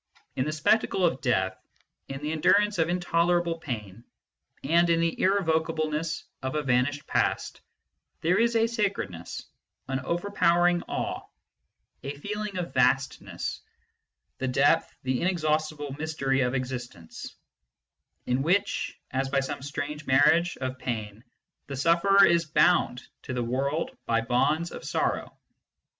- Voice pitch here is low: No, medium, 150 Hz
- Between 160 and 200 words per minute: No, average, 140 wpm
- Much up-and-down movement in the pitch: No, average, 4.8 semitones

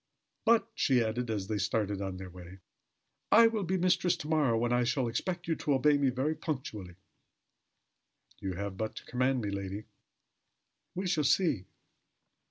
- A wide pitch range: Yes, wide, 7.5 semitones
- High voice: No, low, 125 Hz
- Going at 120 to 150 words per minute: No, average, 170 wpm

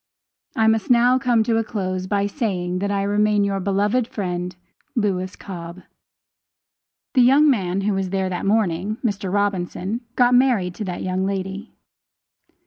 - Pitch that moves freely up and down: No, average, 3.1 semitones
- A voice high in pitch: Yes, high, 200 Hz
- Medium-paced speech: Yes, average, 155 wpm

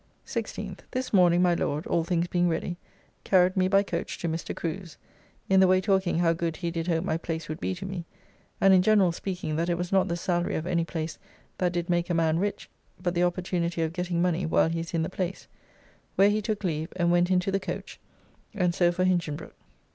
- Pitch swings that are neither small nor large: No, narrow, 1.8 semitones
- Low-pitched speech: No, medium, 175 Hz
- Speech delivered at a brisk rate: Yes, fast, 225 wpm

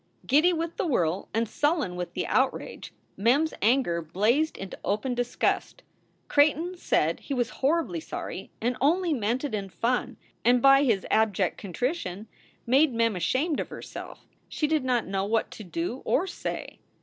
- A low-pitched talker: No, high, 245 Hz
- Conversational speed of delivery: Yes, average, 170 wpm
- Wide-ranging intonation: Yes, wide, 6.7 semitones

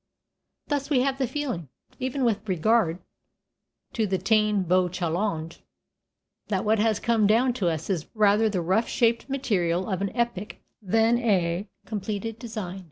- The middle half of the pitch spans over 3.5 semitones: Yes, average, 4.1 semitones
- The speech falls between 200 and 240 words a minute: No, average, 155 wpm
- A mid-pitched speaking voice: No, high, 210 Hz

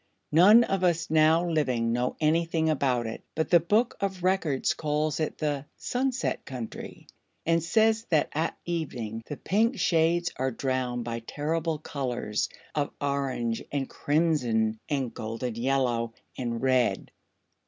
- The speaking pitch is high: No, medium, 150 Hz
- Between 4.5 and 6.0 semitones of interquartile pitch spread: Yes, average, 5.1 semitones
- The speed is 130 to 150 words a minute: Yes, average, 140 wpm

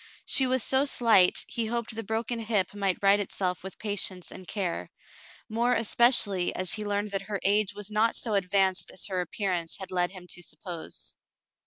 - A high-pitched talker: Yes, high, 205 Hz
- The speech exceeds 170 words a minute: Yes, average, 185 wpm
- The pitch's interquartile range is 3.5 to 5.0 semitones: No, average, 3.1 semitones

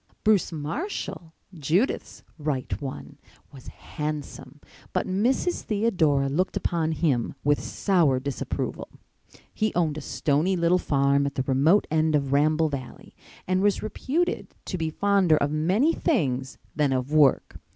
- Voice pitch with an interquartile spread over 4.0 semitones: Yes, average, 4.9 semitones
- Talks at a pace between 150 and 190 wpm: No, average, 140 wpm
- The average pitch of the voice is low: No, medium, 155 Hz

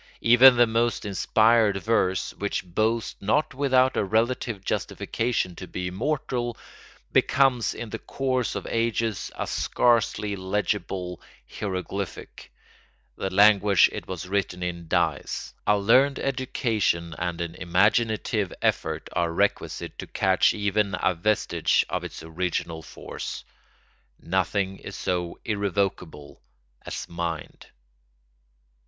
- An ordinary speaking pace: No, slow, 115 wpm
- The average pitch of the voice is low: Yes, low, 100 Hz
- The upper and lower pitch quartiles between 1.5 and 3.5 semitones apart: No, average, 4.2 semitones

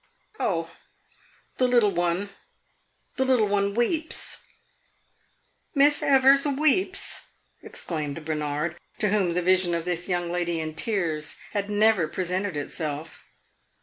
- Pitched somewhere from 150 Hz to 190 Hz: Yes, medium, 185 Hz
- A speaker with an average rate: No, slow, 115 wpm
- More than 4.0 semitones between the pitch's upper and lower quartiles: Yes, wide, 5.6 semitones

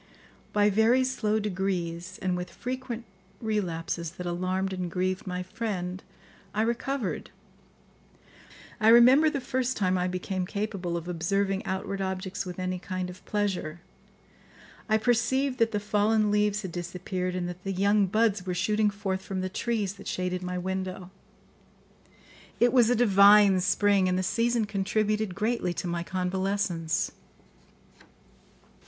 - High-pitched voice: Yes, high, 195 Hz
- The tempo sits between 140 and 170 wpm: Yes, average, 145 wpm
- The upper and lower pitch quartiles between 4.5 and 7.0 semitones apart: No, average, 3.0 semitones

